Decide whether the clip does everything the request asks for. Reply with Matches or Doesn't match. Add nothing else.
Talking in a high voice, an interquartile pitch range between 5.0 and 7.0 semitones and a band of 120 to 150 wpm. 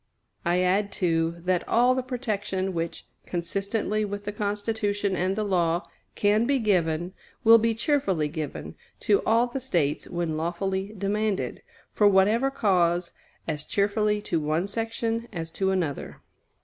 Doesn't match